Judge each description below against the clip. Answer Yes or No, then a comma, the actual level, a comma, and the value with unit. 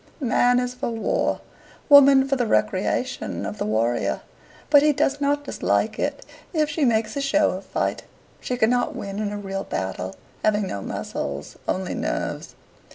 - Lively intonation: Yes, wide, 6.4 semitones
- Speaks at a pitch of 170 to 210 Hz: No, high, 235 Hz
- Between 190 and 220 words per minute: No, average, 165 wpm